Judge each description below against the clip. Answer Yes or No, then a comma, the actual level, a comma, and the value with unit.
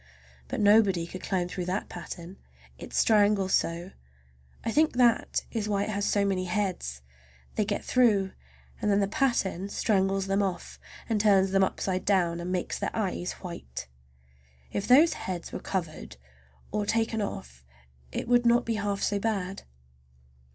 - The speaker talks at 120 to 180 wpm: Yes, average, 160 wpm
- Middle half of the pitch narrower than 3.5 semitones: Yes, average, 2.8 semitones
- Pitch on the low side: No, high, 195 Hz